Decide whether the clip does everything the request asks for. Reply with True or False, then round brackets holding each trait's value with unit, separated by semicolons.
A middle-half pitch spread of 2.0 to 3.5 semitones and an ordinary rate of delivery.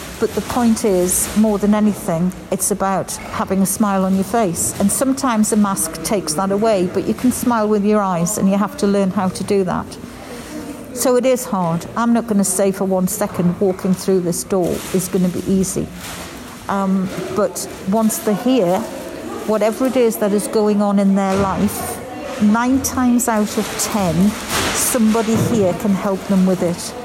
True (2.8 semitones; 190 wpm)